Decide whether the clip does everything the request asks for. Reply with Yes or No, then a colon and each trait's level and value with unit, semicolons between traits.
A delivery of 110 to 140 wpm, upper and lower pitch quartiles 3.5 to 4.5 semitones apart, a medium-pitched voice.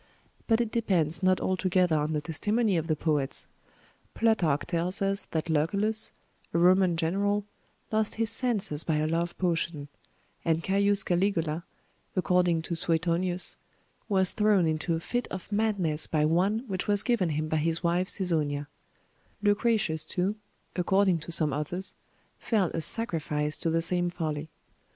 No: average, 150 wpm; average, 3.9 semitones; medium, 175 Hz